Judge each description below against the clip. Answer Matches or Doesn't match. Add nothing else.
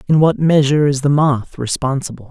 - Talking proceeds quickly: Doesn't match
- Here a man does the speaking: Matches